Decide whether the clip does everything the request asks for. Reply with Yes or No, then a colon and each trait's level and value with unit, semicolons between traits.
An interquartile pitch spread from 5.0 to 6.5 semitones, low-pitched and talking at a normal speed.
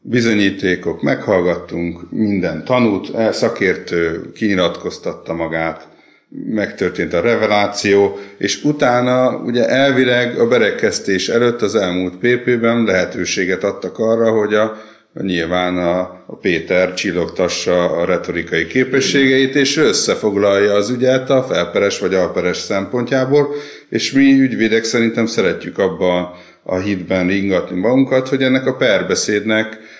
Yes: wide, 5.4 semitones; low, 110 Hz; average, 115 wpm